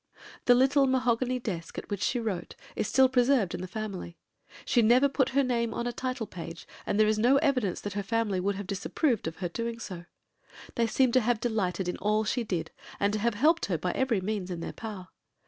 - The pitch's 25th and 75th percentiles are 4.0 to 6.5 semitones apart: Yes, average, 4.6 semitones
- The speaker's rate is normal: No, fast, 225 wpm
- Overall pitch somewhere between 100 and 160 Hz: No, high, 220 Hz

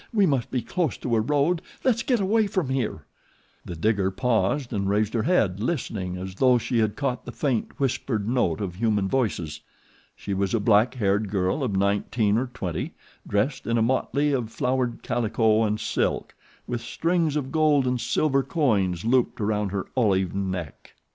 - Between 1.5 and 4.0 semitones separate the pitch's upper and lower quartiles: No, average, 5.1 semitones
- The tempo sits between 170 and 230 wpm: Yes, average, 180 wpm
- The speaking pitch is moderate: No, low, 115 Hz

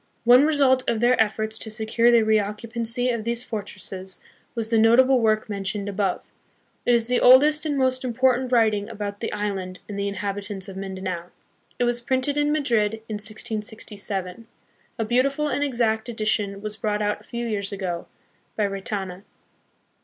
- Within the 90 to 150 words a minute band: No, average, 165 wpm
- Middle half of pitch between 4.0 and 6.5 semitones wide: No, average, 3.1 semitones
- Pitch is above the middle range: Yes, high, 220 Hz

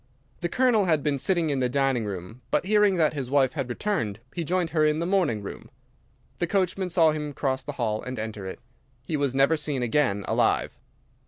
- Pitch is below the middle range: No, medium, 145 Hz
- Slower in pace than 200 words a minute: No, fast, 205 wpm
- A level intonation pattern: No, wide, 5.4 semitones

